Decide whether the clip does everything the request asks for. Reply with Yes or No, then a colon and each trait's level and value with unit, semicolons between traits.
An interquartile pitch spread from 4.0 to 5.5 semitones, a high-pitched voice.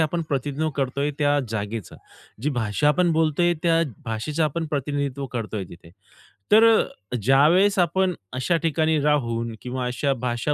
No: average, 4.6 semitones; medium, 145 Hz